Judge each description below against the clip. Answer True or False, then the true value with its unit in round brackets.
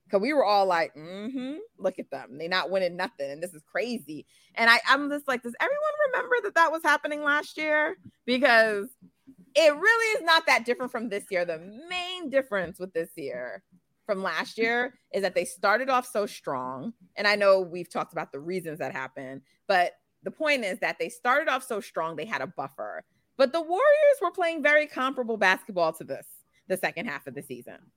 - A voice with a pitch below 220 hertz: False (230 Hz)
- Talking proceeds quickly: True (210 wpm)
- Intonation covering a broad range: True (8.7 semitones)